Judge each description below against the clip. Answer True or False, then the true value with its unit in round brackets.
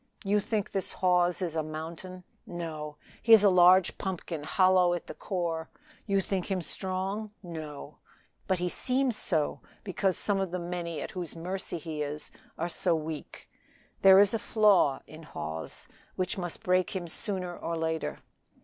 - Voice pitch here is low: False (180 Hz)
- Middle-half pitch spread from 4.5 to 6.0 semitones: False (2.9 semitones)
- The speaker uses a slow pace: False (165 wpm)